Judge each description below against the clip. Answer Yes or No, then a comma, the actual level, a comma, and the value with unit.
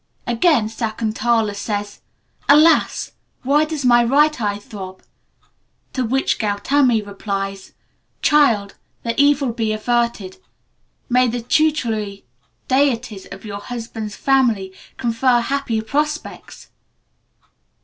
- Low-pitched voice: No, high, 235 Hz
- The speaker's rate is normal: No, slow, 100 wpm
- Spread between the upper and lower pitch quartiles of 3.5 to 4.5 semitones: Yes, average, 4.2 semitones